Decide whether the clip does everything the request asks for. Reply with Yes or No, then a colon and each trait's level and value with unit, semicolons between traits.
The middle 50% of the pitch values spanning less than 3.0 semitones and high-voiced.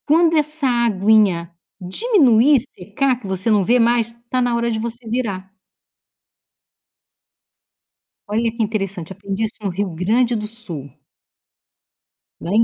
No: average, 3.8 semitones; high, 225 Hz